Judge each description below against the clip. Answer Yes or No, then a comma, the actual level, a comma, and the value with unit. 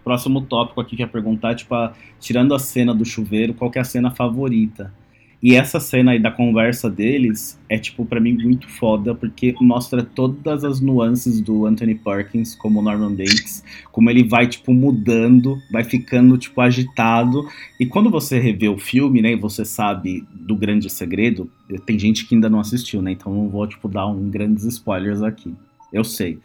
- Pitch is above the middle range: No, low, 115 Hz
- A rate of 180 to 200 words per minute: Yes, fast, 185 wpm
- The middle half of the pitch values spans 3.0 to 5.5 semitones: No, narrow, 2.5 semitones